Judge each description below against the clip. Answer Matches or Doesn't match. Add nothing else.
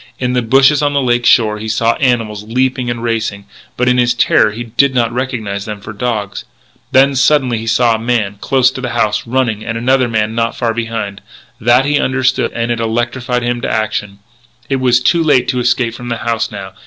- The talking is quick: Matches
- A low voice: Matches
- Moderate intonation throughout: Doesn't match